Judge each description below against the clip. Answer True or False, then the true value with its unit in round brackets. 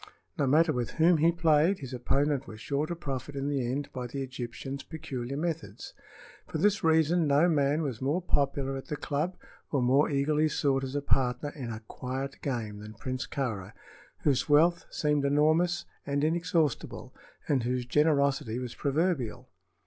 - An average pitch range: True (3.3 semitones)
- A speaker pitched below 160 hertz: True (140 Hz)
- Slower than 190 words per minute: True (170 wpm)